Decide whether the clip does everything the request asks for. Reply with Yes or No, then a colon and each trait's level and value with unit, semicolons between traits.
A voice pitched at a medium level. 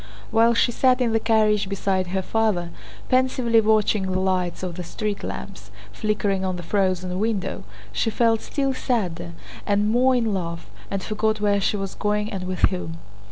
No: high, 205 Hz